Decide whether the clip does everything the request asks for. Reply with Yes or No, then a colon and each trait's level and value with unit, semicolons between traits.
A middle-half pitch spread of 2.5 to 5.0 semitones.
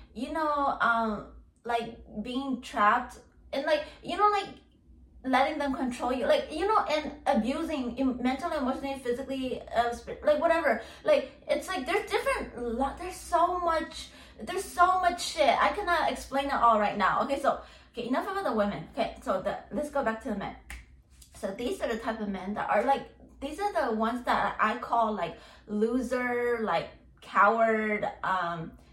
No: wide, 5.4 semitones